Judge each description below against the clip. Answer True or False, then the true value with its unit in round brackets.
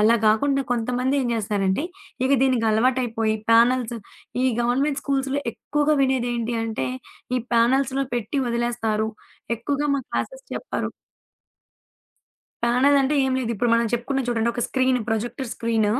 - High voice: True (240 Hz)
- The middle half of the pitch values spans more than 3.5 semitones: False (2.8 semitones)